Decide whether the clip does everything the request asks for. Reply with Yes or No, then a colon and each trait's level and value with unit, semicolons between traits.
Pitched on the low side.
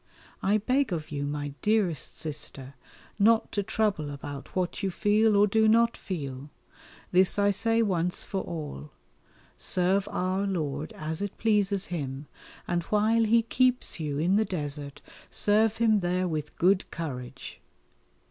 No: medium, 185 Hz